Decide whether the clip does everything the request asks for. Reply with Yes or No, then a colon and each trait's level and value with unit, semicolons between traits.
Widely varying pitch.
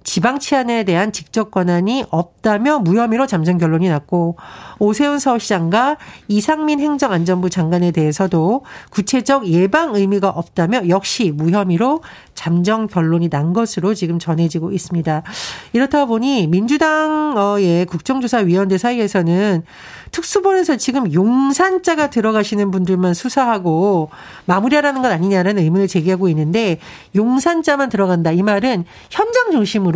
Yes: wide, 6.8 semitones